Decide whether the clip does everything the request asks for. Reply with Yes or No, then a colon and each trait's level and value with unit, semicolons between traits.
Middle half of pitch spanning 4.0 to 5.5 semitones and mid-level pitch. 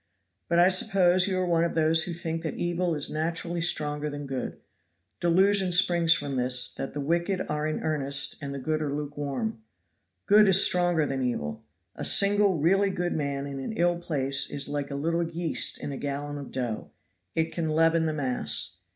No: average, 3.6 semitones; medium, 160 Hz